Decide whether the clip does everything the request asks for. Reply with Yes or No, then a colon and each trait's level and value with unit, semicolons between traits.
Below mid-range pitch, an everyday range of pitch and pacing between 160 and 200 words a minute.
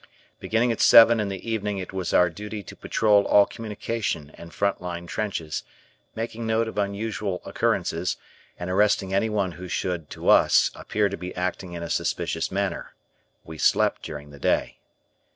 Yes: low, 100 Hz; average, 3.2 semitones; average, 170 wpm